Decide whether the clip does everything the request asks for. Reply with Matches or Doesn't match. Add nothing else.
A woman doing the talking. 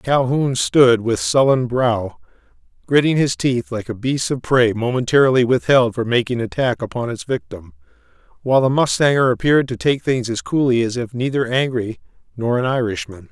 Doesn't match